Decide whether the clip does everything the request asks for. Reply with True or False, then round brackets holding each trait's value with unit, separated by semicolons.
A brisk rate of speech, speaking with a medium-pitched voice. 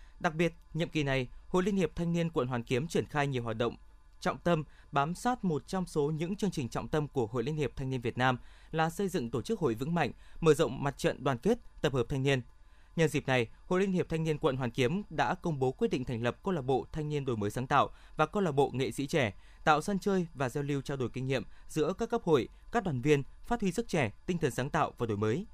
True (275 wpm; 150 Hz)